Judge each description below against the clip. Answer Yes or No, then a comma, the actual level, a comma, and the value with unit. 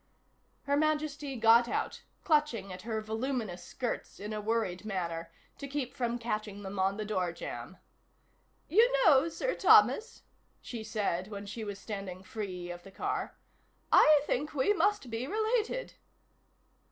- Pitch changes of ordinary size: No, wide, 6.5 semitones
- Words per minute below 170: Yes, average, 150 wpm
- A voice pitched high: Yes, high, 225 Hz